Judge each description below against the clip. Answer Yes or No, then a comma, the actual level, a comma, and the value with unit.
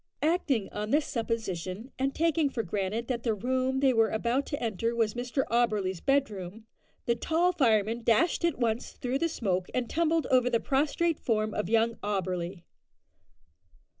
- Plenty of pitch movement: No, average, 4.3 semitones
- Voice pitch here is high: Yes, high, 235 Hz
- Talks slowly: No, average, 165 wpm